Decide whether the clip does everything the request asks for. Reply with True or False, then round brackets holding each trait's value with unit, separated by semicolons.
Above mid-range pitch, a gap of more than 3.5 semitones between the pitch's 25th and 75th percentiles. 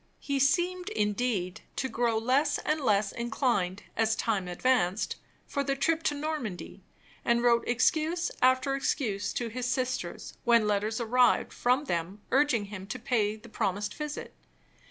True (235 Hz; 4.7 semitones)